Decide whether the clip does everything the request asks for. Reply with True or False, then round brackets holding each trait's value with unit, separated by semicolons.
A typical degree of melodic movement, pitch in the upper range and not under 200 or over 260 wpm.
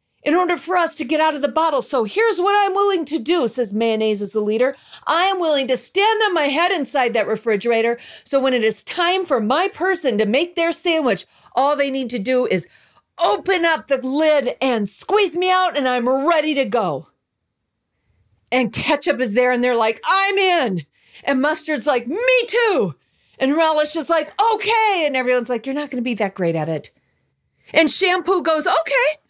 False (6.4 semitones; 290 Hz; 205 wpm)